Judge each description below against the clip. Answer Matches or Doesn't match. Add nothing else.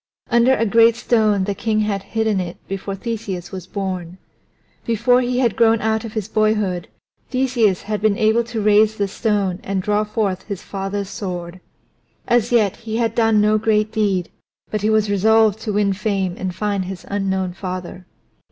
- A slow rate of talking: Doesn't match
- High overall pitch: Matches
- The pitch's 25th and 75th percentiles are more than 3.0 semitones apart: Doesn't match